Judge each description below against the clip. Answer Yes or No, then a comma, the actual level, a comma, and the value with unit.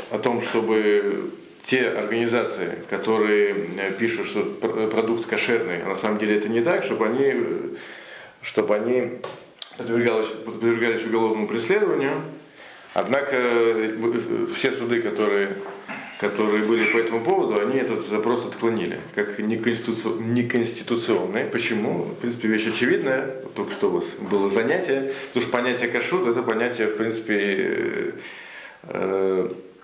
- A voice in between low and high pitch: No, low, 115 Hz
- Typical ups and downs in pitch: No, narrow, 2.3 semitones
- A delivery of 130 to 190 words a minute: No, average, 120 wpm